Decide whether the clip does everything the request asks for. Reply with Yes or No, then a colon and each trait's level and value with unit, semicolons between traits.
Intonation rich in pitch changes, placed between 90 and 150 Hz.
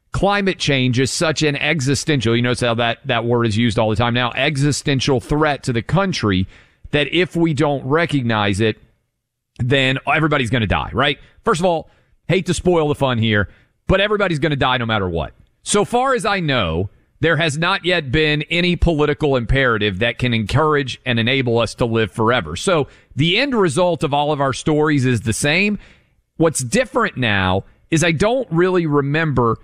Yes: wide, 5.8 semitones; medium, 140 Hz